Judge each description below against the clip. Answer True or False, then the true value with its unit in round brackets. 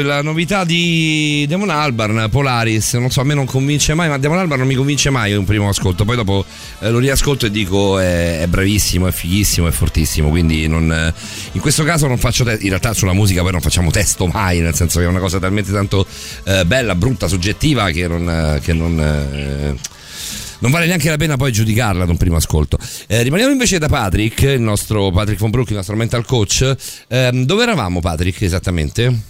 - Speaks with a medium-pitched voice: False (105 Hz)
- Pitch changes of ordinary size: False (6.7 semitones)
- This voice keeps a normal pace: False (210 wpm)